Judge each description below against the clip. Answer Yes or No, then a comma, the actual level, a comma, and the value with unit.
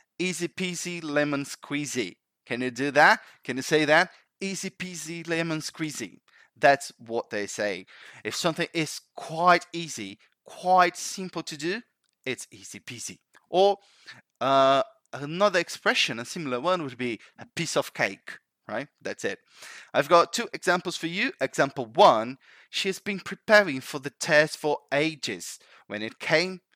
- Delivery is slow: No, average, 150 wpm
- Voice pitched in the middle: Yes, medium, 165 Hz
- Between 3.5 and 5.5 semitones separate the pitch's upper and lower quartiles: Yes, average, 4.2 semitones